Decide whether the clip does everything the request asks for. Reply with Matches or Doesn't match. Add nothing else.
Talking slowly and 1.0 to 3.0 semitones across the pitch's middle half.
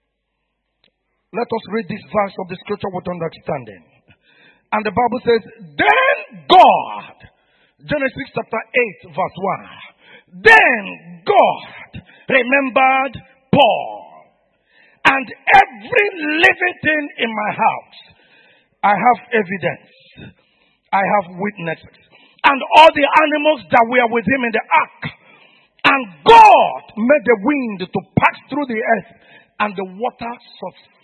Doesn't match